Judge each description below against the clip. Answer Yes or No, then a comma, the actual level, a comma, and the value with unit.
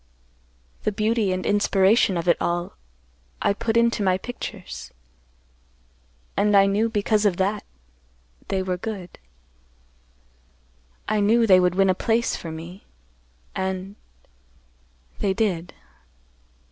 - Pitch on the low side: No, medium, 185 Hz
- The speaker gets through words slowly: Yes, slow, 110 wpm